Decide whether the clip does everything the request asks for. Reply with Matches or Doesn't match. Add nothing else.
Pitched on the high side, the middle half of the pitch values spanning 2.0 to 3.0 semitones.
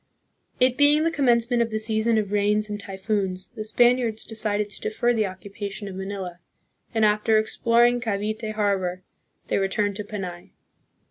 Matches